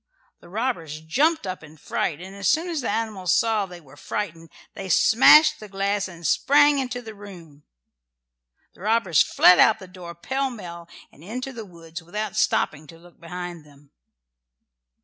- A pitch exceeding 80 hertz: Yes, high, 190 Hz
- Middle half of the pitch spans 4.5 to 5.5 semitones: Yes, average, 5.2 semitones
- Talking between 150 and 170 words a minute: No, average, 180 wpm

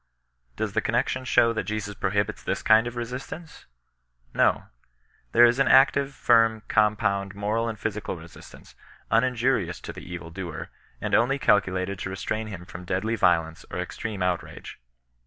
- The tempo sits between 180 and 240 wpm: No, average, 155 wpm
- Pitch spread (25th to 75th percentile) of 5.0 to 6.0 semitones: No, average, 3.8 semitones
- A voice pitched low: Yes, low, 110 Hz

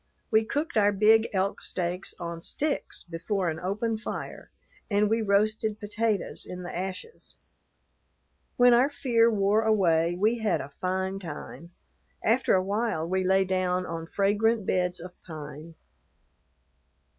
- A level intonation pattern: No, average, 3.5 semitones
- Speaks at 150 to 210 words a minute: No, average, 140 wpm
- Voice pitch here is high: Yes, high, 195 Hz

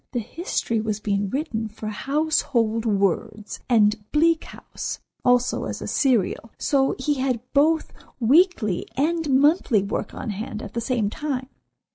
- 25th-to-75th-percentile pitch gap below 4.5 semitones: No, average, 5.2 semitones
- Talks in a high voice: Yes, high, 245 Hz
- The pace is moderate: Yes, average, 145 wpm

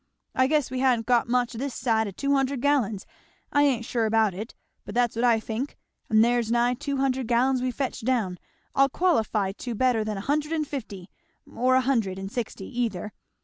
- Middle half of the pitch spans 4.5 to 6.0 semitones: No, average, 3.2 semitones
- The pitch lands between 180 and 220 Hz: No, high, 245 Hz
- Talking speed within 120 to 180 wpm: No, fast, 205 wpm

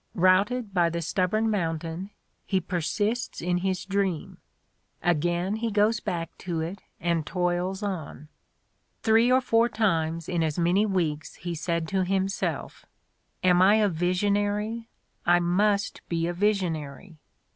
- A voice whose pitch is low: No, medium, 185 Hz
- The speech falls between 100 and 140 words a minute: Yes, slow, 135 wpm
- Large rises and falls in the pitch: No, average, 3.4 semitones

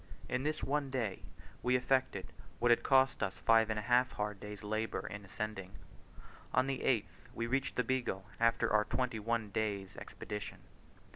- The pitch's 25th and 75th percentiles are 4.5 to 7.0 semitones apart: No, average, 3.6 semitones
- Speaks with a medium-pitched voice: No, low, 115 Hz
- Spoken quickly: No, average, 170 wpm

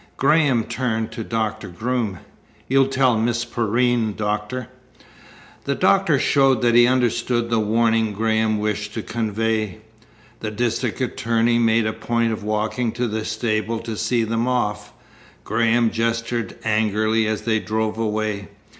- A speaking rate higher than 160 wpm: No, average, 140 wpm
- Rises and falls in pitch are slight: Yes, narrow, 1.7 semitones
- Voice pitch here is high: No, low, 115 Hz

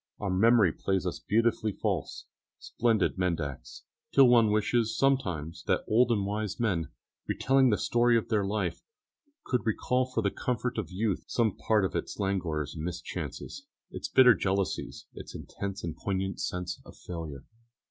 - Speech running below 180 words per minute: Yes, average, 155 wpm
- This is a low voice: Yes, low, 105 Hz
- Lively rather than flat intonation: No, average, 4.3 semitones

